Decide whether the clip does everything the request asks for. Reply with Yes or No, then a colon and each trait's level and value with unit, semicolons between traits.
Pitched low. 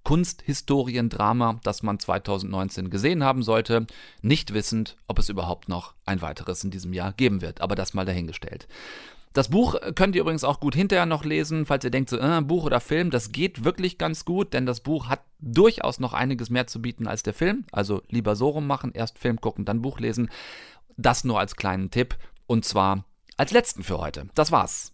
Yes: low, 120 Hz